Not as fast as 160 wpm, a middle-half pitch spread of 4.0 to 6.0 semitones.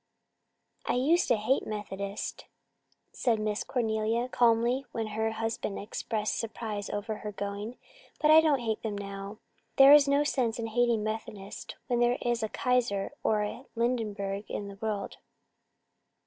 No: average, 150 wpm; average, 2.7 semitones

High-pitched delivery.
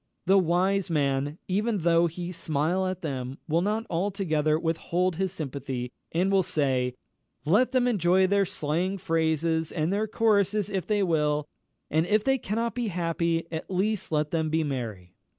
No: medium, 170 Hz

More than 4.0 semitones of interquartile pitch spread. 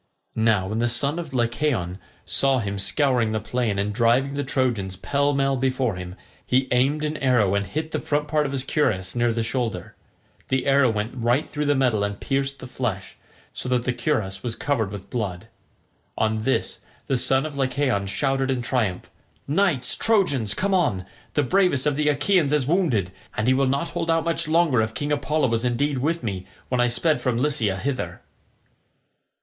Yes: average, 4.6 semitones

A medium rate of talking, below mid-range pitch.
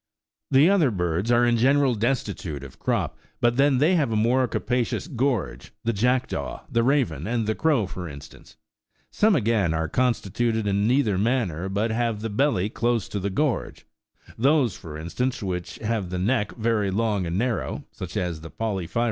Yes: average, 180 wpm; low, 115 Hz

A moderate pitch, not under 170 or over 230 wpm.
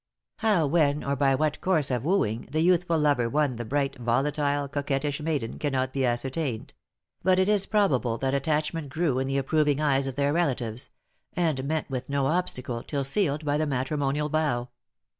Yes: medium, 145 Hz; average, 180 wpm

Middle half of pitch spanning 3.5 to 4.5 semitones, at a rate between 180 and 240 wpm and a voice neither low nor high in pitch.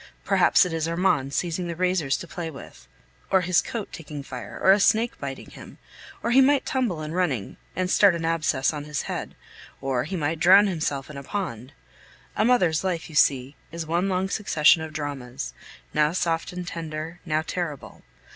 Yes: average, 3.9 semitones; average, 190 wpm; medium, 165 Hz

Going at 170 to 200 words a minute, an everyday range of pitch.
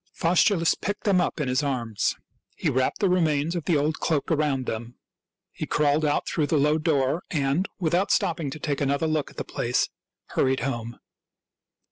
Yes: average, 180 wpm; average, 3.4 semitones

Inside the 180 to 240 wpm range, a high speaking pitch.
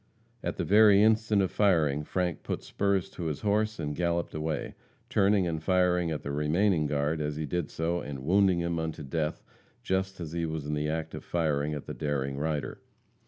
No: average, 200 wpm; very low, 80 Hz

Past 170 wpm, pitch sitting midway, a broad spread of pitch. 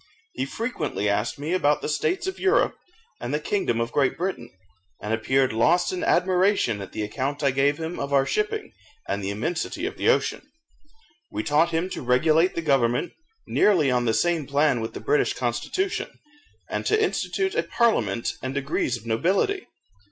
Yes: average, 180 wpm; medium, 145 Hz; wide, 7.5 semitones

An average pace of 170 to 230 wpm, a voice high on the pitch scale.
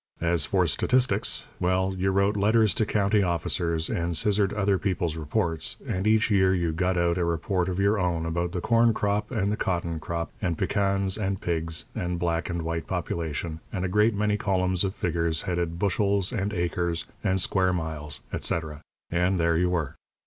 No: average, 185 wpm; very low, 90 Hz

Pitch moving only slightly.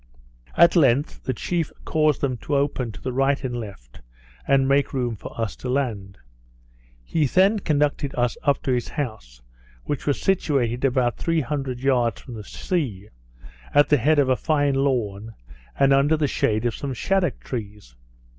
No: average, 3.7 semitones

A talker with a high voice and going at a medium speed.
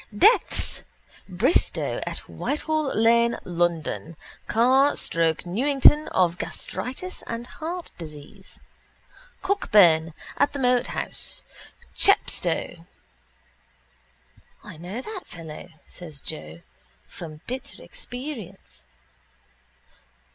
No: high, 225 Hz; slow, 85 wpm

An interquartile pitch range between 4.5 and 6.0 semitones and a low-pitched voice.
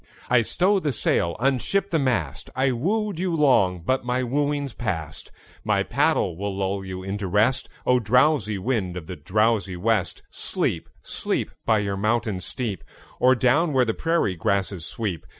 Yes: wide, 5.5 semitones; low, 115 Hz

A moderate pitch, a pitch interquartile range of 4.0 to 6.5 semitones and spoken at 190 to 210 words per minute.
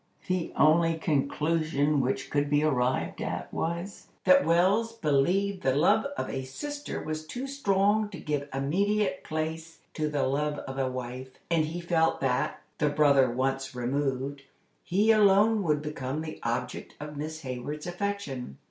No: medium, 155 Hz; average, 5.2 semitones; average, 155 wpm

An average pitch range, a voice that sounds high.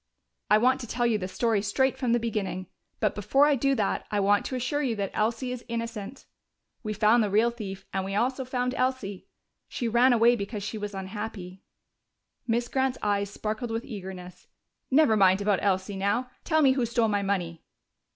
Yes: average, 3.6 semitones; high, 220 Hz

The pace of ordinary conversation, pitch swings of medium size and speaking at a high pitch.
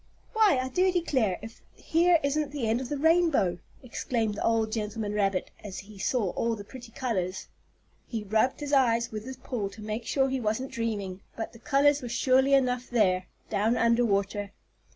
Yes: average, 190 wpm; average, 4.1 semitones; high, 230 Hz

